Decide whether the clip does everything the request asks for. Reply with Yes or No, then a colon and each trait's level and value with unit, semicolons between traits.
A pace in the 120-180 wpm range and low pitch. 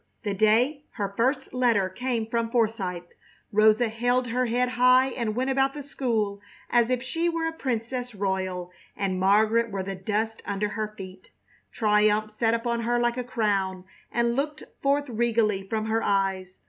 No: average, 170 wpm; high, 225 Hz